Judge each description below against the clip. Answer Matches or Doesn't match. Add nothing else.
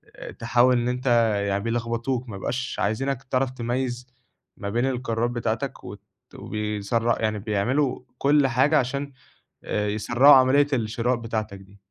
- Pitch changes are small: Doesn't match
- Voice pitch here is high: Doesn't match